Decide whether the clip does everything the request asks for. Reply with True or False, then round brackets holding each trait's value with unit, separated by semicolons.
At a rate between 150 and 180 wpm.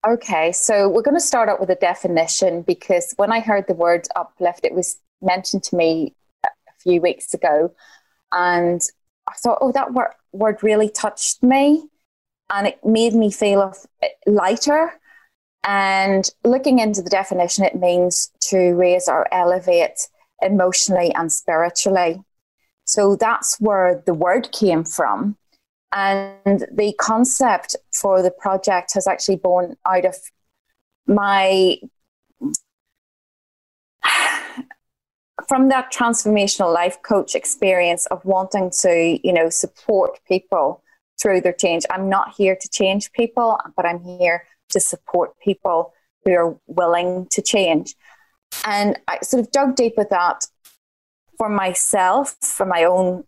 False (140 wpm)